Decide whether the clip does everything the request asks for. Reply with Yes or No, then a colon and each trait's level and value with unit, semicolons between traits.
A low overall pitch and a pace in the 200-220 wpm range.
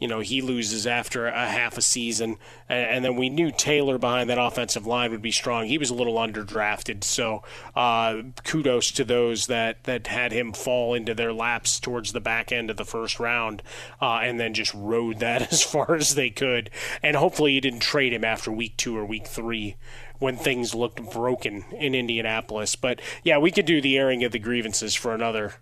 Yes: low, 120 Hz; fast, 205 wpm